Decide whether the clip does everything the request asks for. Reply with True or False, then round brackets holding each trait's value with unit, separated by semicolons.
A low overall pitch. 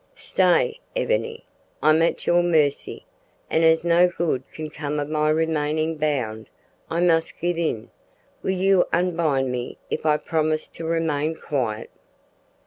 False (160 Hz)